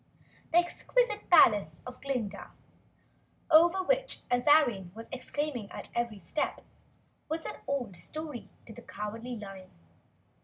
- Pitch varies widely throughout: Yes, wide, 6.9 semitones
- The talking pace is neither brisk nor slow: No, slow, 120 wpm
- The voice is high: Yes, very high, 250 Hz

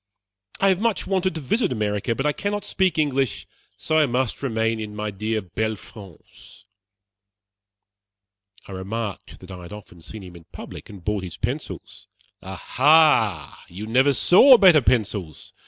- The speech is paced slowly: No, average, 155 wpm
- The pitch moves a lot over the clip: Yes, wide, 7.2 semitones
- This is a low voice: Yes, low, 110 Hz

